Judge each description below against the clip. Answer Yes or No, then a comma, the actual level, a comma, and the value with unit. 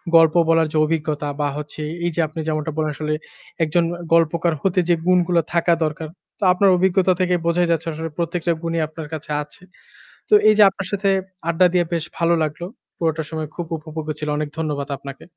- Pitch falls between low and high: Yes, medium, 165 Hz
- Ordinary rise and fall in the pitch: No, narrow, 2.2 semitones